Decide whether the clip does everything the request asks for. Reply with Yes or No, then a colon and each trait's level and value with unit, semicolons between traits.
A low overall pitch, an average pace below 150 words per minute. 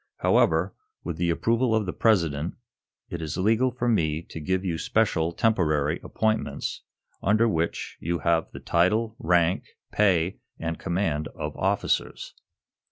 Yes: very low, 90 Hz; average, 140 wpm